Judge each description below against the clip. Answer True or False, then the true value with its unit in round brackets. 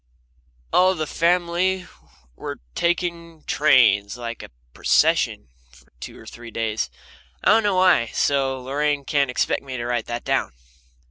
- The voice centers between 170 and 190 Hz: False (140 Hz)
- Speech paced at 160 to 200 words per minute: False (145 wpm)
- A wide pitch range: True (6.4 semitones)